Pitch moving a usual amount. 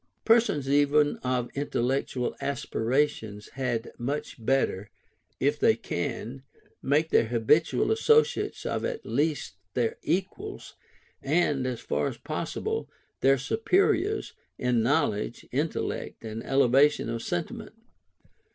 Yes: average, 4.5 semitones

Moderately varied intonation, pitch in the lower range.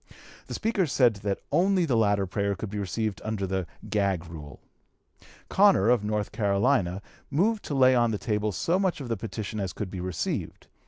Yes: average, 4.2 semitones; low, 105 Hz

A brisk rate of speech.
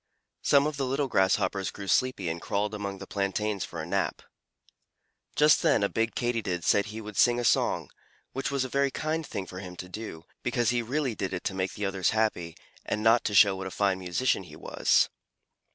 Yes: fast, 215 wpm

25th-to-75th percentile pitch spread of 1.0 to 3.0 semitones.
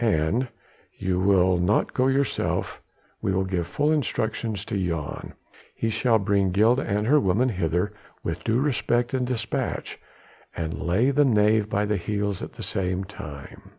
No: average, 4.5 semitones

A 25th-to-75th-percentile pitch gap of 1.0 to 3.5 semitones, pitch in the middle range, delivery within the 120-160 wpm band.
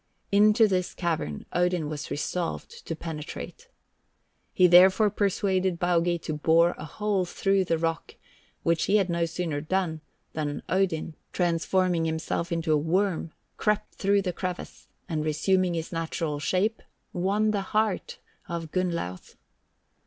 Yes: average, 2.8 semitones; medium, 175 Hz; average, 140 wpm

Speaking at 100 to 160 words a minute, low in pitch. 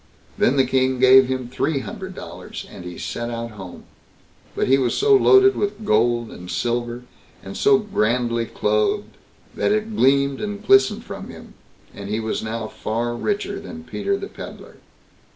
No: average, 170 wpm; low, 130 Hz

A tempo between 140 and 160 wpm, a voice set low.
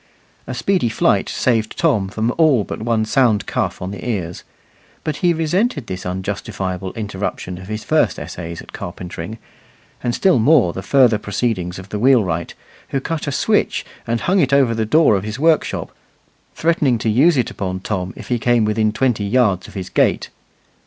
No: average, 180 wpm; low, 110 Hz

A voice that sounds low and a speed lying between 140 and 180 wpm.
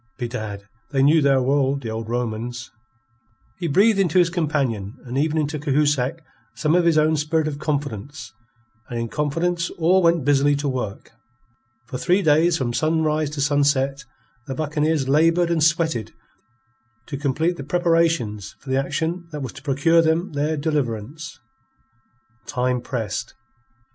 No: medium, 145 Hz; average, 150 wpm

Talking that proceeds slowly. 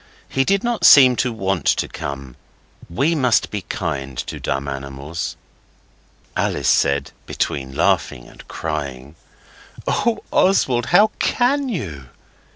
Yes: slow, 125 wpm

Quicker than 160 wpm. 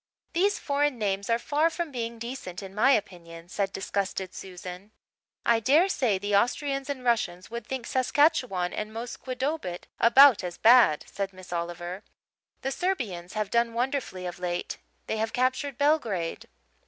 No: average, 155 wpm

